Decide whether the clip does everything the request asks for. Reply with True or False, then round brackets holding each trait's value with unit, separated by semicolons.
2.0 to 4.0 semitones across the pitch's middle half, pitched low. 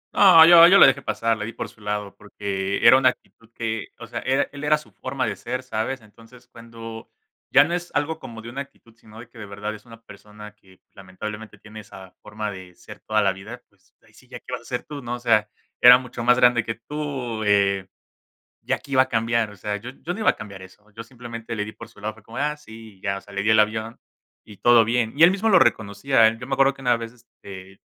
True (3.3 semitones; 115 Hz)